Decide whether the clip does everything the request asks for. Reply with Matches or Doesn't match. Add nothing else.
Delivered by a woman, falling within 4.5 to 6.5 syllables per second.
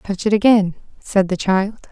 Doesn't match